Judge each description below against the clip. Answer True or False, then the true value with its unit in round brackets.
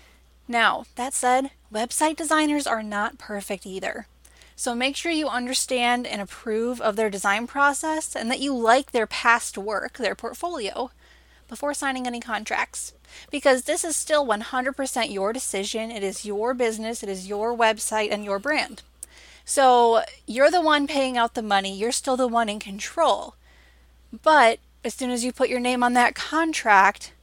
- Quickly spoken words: False (170 wpm)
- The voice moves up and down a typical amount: True (4.1 semitones)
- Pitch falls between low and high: False (245 Hz)